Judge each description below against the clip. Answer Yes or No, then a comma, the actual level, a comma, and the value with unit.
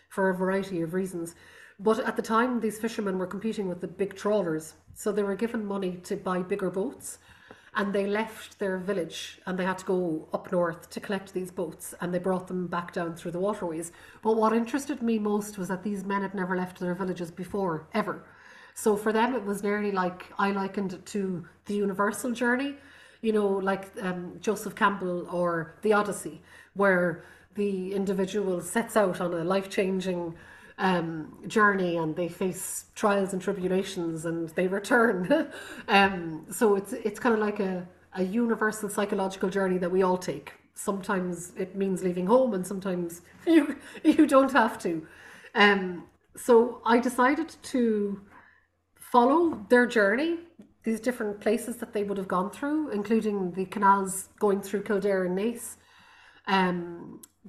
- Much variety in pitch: No, average, 3.1 semitones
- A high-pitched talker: Yes, high, 200 Hz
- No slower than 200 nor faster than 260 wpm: No, average, 170 wpm